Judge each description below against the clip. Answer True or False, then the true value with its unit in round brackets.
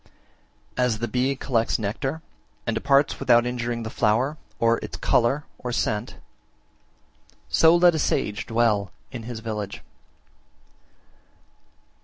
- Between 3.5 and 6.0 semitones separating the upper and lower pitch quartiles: False (3.1 semitones)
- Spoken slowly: True (125 wpm)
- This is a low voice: True (120 Hz)